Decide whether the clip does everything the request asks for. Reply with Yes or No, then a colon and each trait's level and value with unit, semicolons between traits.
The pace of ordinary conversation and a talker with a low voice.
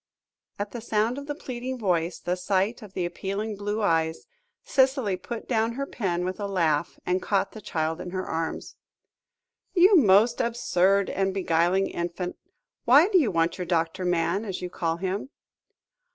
No: average, 170 wpm; high, 195 Hz